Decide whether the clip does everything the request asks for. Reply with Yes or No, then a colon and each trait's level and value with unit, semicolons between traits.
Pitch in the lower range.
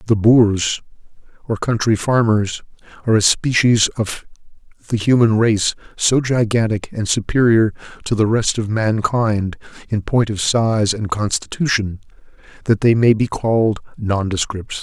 Yes: low, 110 Hz